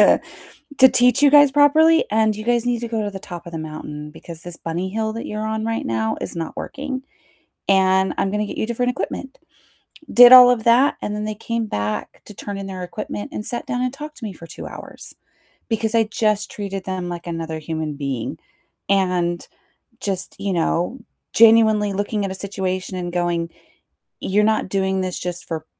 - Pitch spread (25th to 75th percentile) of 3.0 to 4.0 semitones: No, average, 4.6 semitones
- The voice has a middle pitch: No, high, 200 Hz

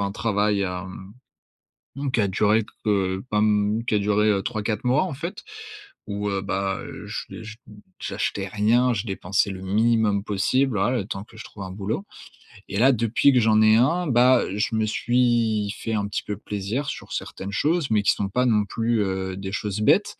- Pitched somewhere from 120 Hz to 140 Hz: No, low, 105 Hz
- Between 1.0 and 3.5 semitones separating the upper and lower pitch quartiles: Yes, average, 2.9 semitones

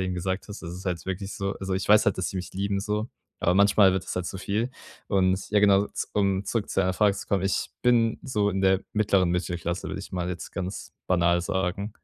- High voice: No, very low, 95 Hz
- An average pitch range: No, narrow, 1.8 semitones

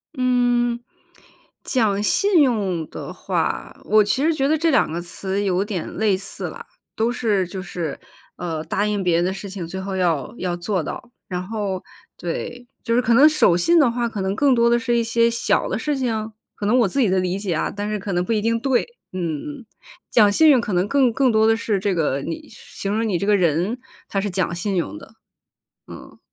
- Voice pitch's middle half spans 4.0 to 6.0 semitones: Yes, average, 4.5 semitones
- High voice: Yes, high, 210 Hz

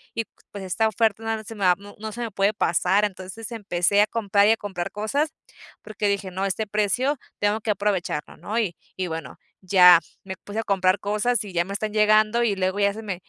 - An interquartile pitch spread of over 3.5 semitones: No, narrow, 2.4 semitones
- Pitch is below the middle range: No, high, 205 Hz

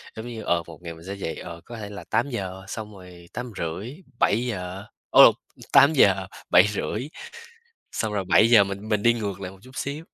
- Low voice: Yes, low, 100 Hz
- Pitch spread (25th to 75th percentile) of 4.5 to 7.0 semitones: No, average, 4.1 semitones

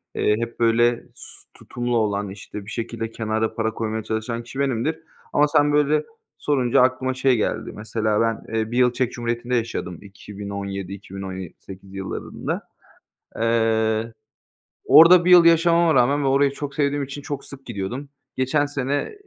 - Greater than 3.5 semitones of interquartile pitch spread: Yes, average, 4.2 semitones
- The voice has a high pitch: No, low, 120 Hz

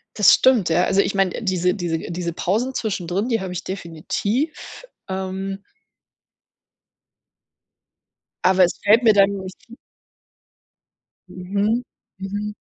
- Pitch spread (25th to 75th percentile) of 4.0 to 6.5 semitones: No, narrow, 2.5 semitones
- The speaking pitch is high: Yes, high, 195 Hz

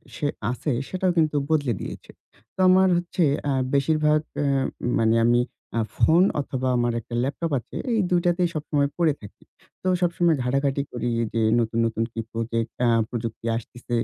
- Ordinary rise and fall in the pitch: No, wide, 5.9 semitones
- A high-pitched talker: No, medium, 140 Hz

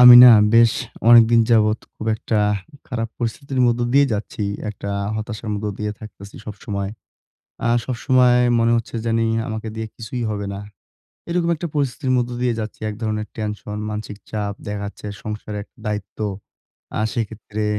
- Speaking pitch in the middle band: No, low, 110 Hz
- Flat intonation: Yes, narrow, 2.1 semitones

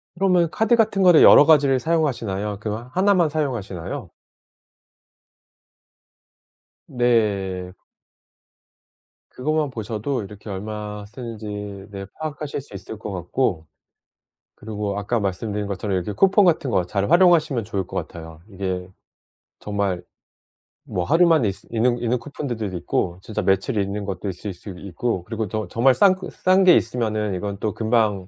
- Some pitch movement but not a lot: No, wide, 5.7 semitones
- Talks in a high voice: No, low, 110 Hz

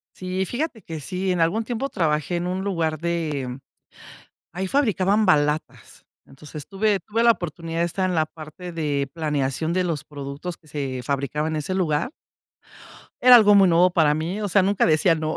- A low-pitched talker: No, medium, 170 Hz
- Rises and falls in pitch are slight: No, average, 3.9 semitones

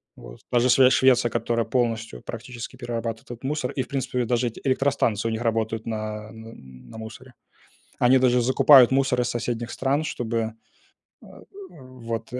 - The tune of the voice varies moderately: No, narrow, 2.3 semitones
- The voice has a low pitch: Yes, low, 120 Hz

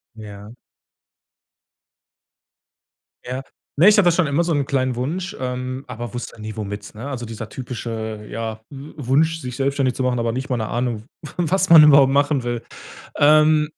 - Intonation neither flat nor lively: Yes, average, 4.3 semitones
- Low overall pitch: Yes, low, 130 Hz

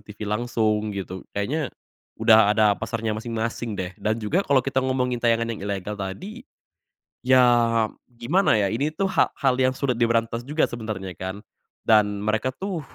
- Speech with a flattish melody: No, average, 3.6 semitones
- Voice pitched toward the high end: No, low, 115 Hz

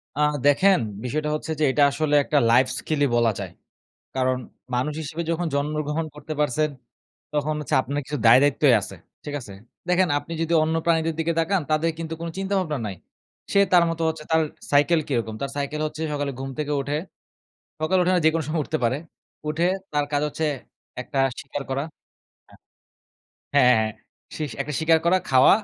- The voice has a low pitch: No, medium, 150 Hz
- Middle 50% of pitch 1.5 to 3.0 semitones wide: Yes, narrow, 2.5 semitones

